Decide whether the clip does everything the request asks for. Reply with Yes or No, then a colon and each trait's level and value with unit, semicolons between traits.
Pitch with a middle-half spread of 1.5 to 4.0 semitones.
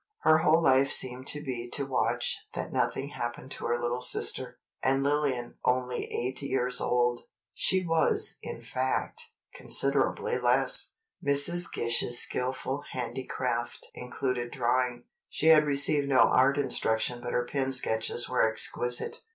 Yes: narrow, 2.5 semitones